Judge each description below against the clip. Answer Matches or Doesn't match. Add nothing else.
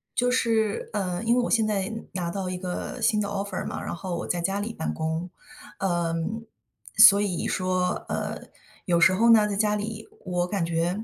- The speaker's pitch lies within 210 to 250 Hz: Doesn't match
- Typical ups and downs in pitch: Matches